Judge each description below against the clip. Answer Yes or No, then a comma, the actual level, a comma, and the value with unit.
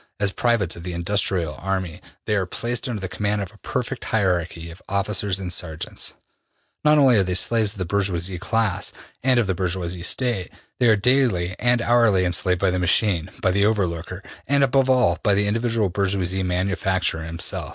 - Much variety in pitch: No, average, 3.9 semitones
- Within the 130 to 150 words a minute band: No, average, 190 wpm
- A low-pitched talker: Yes, low, 100 Hz